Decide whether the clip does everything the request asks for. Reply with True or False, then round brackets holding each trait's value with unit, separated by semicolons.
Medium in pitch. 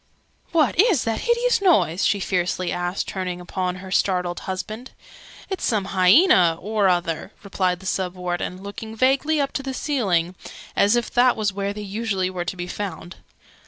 False (195 Hz)